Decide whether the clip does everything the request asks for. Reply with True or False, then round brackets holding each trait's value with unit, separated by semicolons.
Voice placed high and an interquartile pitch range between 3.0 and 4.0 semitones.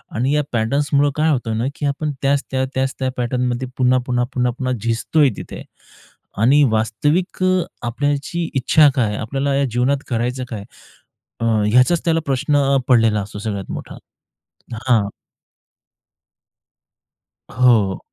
False (130 Hz; 3.6 semitones)